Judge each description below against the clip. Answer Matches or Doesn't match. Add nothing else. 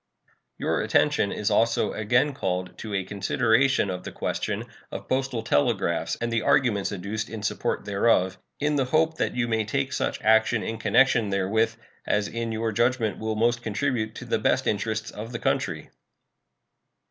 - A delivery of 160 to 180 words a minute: Matches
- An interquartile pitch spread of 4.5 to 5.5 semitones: Doesn't match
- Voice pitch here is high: Doesn't match